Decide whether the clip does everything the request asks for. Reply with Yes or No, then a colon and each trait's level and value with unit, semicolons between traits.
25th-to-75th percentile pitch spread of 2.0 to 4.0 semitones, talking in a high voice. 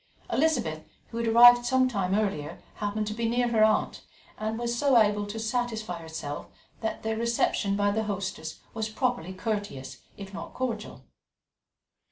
Yes: average, 2.8 semitones; high, 215 Hz